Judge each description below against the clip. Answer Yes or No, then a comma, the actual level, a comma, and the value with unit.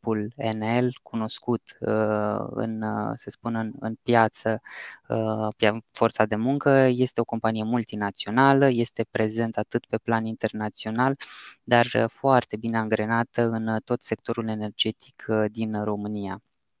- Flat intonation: Yes, narrow, 1.6 semitones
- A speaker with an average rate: No, slow, 110 wpm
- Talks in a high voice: No, low, 110 Hz